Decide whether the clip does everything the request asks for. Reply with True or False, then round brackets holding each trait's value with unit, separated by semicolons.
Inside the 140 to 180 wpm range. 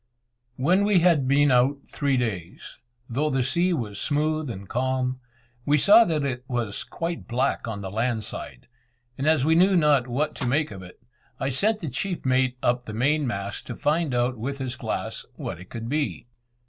False (195 wpm)